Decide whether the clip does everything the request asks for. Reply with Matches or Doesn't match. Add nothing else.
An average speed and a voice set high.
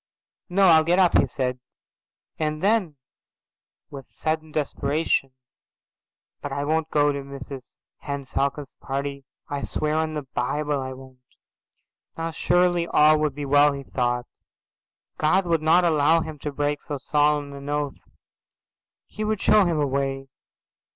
Doesn't match